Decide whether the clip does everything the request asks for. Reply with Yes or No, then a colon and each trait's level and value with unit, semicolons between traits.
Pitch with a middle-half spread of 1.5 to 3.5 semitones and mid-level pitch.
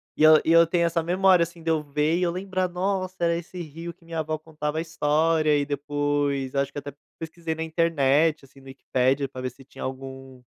Yes: average, 2.9 semitones; medium, 155 Hz